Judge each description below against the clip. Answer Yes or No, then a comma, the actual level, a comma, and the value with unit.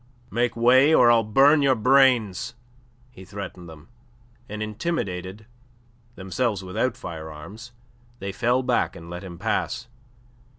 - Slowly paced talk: Yes, slow, 125 wpm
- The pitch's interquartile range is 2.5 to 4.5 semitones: No, average, 5.1 semitones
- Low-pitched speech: Yes, low, 110 Hz